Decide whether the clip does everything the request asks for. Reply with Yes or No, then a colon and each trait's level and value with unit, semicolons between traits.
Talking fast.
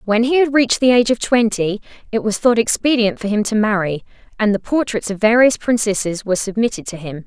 Yes: fast, 215 wpm